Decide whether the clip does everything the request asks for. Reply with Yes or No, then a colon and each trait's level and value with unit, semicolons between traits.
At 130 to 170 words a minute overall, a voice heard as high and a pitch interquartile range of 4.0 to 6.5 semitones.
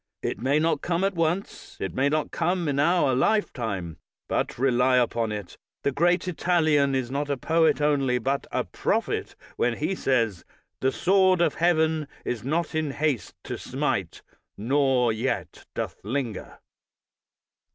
No: average, 150 wpm; medium, 140 Hz; average, 4.8 semitones